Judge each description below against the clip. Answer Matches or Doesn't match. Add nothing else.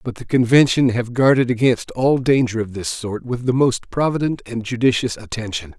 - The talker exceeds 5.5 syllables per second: Doesn't match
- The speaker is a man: Matches